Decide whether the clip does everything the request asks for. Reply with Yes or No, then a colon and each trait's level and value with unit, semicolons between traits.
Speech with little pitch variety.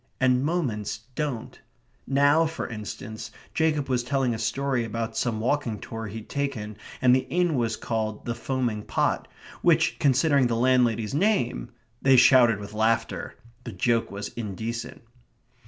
No: average, 3.6 semitones